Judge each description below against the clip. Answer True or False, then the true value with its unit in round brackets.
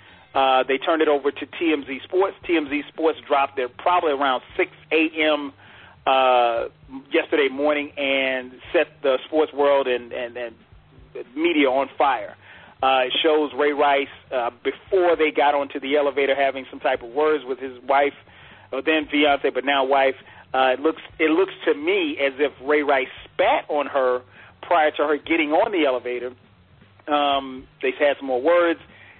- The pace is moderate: True (170 wpm)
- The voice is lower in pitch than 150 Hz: True (140 Hz)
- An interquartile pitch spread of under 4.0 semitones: True (2.8 semitones)